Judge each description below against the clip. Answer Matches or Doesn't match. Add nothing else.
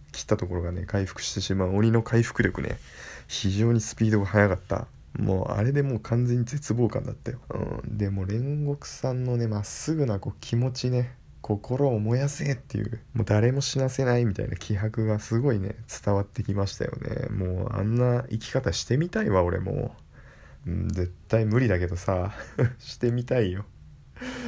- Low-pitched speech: Matches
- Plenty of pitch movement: Doesn't match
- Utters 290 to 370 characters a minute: Matches